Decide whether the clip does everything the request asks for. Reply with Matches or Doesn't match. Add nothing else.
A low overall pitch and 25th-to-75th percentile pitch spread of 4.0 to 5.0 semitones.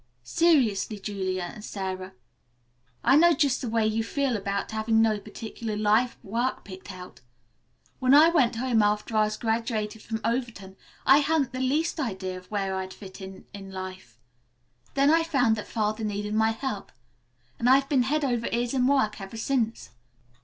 Doesn't match